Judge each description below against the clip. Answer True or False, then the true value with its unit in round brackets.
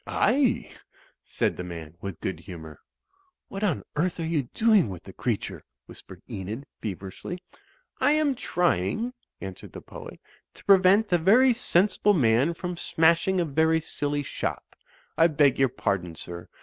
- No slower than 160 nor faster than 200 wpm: False (150 wpm)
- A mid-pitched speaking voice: True (160 Hz)